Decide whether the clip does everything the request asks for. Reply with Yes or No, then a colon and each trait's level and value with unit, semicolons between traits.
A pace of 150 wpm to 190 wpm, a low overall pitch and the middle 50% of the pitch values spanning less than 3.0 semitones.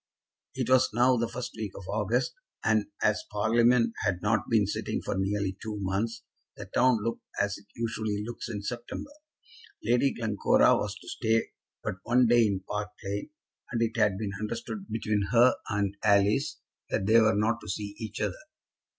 Yes: average, 175 wpm; low, 110 Hz; narrow, 2.4 semitones